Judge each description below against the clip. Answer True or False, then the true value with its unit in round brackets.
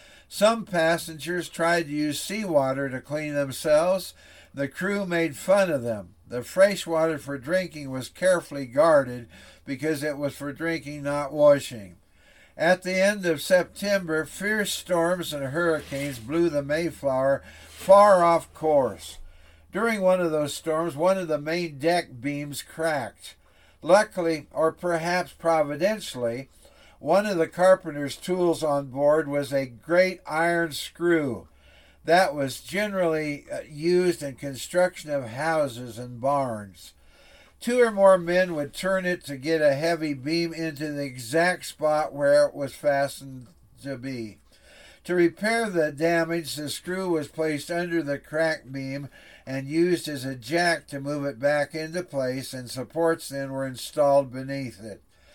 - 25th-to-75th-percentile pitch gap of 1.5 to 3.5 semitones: False (4.0 semitones)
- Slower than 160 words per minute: True (145 wpm)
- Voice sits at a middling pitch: True (150 Hz)